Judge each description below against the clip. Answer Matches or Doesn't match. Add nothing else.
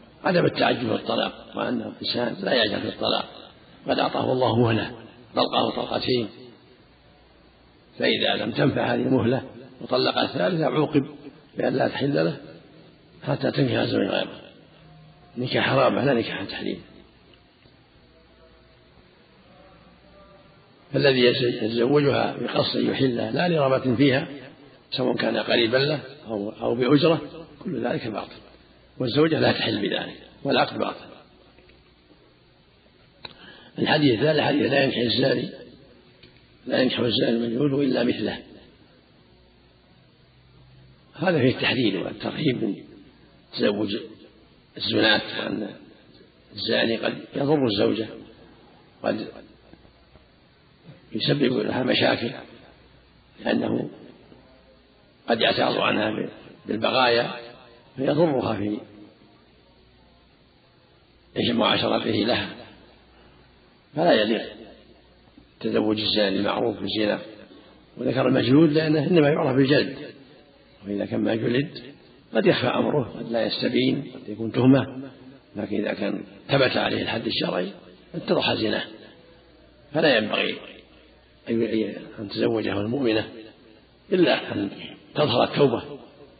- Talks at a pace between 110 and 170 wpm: Doesn't match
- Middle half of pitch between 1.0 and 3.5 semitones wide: Doesn't match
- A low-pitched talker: Matches